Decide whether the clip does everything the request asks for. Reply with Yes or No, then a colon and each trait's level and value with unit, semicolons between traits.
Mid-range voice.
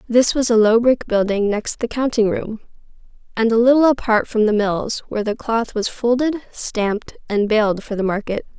No: high, 225 Hz